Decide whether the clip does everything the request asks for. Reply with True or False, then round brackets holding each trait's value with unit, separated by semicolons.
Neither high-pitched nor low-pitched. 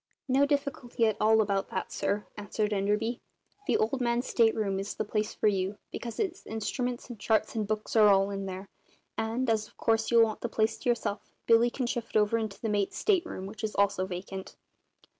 False (220 Hz)